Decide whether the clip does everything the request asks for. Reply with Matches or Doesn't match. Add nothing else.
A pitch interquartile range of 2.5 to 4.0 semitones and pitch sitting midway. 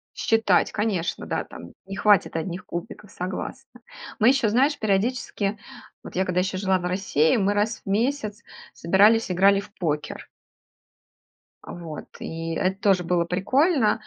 Doesn't match